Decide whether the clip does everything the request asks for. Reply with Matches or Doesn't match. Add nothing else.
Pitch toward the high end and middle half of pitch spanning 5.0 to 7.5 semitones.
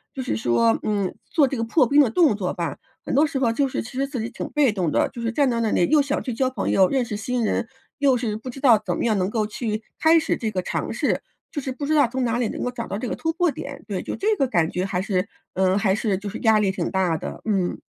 Matches